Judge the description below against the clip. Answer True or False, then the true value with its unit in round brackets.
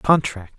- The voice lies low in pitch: True (125 Hz)